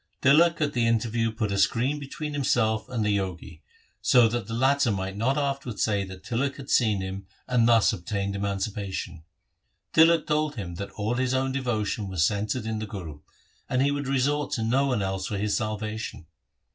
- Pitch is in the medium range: No, low, 115 Hz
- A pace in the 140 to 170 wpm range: No, average, 190 wpm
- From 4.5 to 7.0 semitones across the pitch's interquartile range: Yes, average, 4.9 semitones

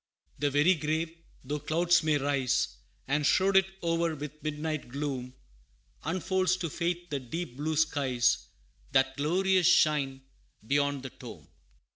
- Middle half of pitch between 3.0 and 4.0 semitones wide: Yes, average, 3.3 semitones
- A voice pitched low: No, medium, 150 Hz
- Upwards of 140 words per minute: No, slow, 135 wpm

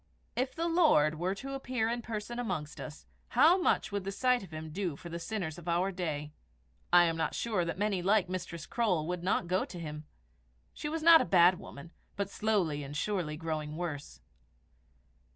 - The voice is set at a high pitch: No, medium, 180 Hz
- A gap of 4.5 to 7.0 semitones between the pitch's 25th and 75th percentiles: Yes, wide, 5.6 semitones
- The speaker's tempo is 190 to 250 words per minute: Yes, average, 195 wpm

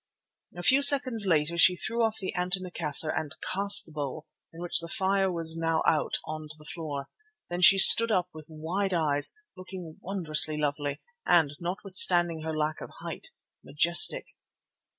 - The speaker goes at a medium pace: Yes, average, 165 wpm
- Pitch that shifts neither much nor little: Yes, average, 3.4 semitones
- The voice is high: No, medium, 170 Hz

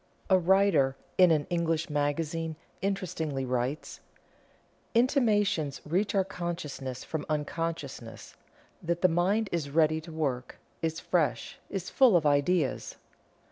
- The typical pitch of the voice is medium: Yes, medium, 165 Hz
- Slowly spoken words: Yes, slow, 120 wpm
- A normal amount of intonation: Yes, average, 3.8 semitones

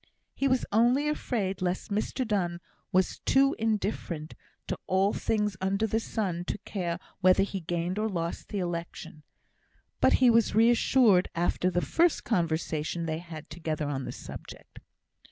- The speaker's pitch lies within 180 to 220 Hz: Yes, high, 190 Hz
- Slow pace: No, average, 155 wpm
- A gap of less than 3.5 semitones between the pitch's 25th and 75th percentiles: No, average, 4.6 semitones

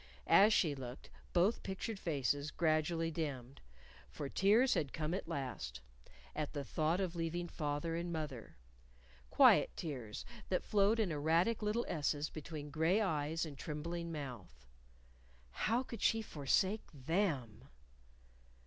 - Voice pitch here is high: No, medium, 160 Hz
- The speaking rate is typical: No, slow, 130 wpm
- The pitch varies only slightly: No, average, 4.1 semitones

